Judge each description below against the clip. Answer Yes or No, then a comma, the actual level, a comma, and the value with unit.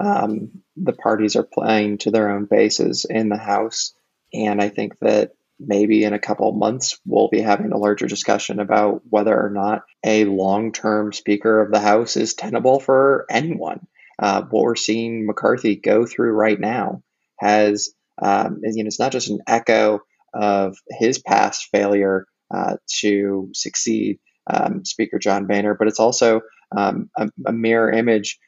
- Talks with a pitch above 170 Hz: No, low, 105 Hz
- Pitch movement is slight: Yes, narrow, 1.4 semitones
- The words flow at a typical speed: Yes, average, 170 wpm